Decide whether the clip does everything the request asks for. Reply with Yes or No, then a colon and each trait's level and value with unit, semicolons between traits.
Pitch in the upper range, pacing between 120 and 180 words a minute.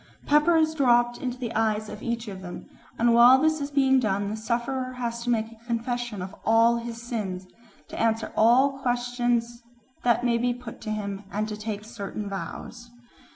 No: high, 235 Hz; average, 190 wpm